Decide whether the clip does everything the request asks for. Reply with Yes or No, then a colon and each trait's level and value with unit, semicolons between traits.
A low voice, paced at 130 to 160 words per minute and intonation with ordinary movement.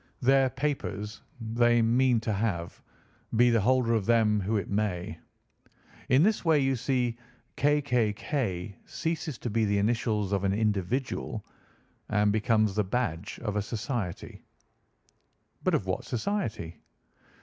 Yes: low, 115 Hz; average, 140 wpm; average, 3.6 semitones